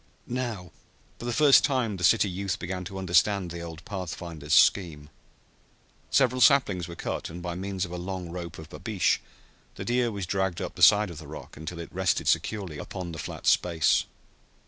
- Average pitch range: Yes, average, 3.2 semitones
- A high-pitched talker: No, very low, 90 Hz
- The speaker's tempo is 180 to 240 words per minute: Yes, average, 190 wpm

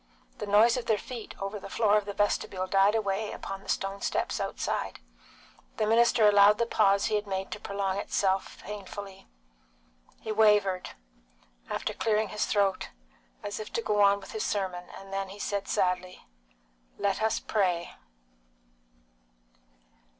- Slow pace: No, average, 155 wpm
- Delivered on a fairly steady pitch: Yes, narrow, 1.5 semitones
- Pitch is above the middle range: Yes, high, 205 Hz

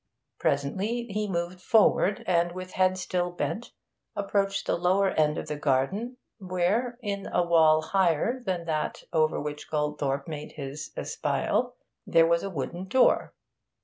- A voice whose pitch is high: No, medium, 175 Hz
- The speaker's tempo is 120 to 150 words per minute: Yes, average, 145 wpm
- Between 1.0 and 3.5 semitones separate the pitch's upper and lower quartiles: No, average, 4.1 semitones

